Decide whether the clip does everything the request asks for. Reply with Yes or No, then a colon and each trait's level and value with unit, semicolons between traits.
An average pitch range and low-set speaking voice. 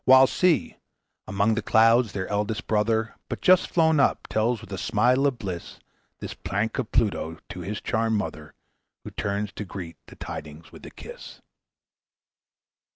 Yes: average, 3.3 semitones; low, 110 Hz